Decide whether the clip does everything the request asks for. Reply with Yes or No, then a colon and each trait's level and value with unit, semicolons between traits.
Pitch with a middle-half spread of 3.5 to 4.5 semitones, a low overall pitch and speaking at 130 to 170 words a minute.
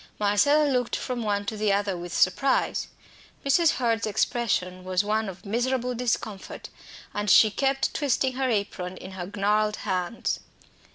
No: average, 4.1 semitones; high, 215 Hz; average, 150 wpm